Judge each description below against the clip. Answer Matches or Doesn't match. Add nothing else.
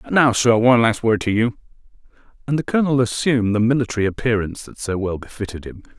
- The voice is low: Matches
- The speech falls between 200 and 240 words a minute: Doesn't match